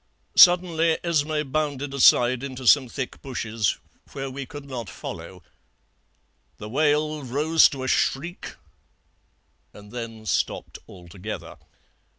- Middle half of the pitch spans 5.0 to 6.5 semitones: No, average, 4.6 semitones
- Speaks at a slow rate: Yes, slow, 115 wpm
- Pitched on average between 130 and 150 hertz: Yes, low, 135 Hz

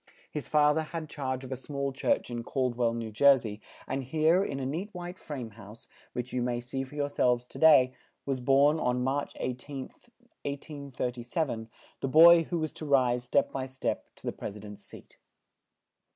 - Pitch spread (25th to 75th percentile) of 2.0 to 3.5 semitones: Yes, average, 3.1 semitones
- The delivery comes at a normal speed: Yes, average, 195 wpm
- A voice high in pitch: No, low, 135 Hz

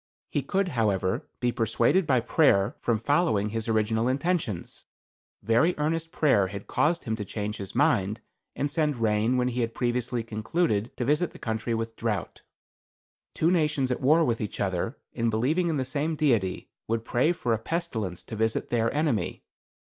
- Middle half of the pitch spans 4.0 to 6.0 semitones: Yes, wide, 5.4 semitones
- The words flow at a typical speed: Yes, average, 175 wpm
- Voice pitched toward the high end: No, low, 120 Hz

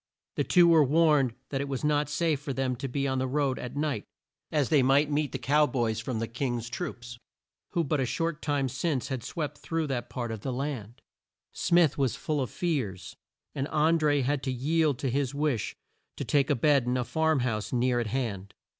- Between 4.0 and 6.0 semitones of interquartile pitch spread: No, average, 3.2 semitones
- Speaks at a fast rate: Yes, fast, 215 wpm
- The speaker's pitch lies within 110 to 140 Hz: Yes, low, 135 Hz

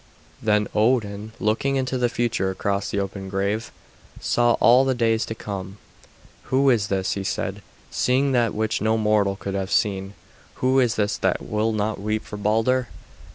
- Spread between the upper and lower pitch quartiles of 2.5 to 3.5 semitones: Yes, average, 3.1 semitones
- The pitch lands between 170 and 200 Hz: No, low, 110 Hz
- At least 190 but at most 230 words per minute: No, average, 170 wpm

